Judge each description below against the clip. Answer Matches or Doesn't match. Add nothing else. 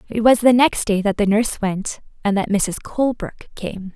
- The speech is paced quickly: Matches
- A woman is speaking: Matches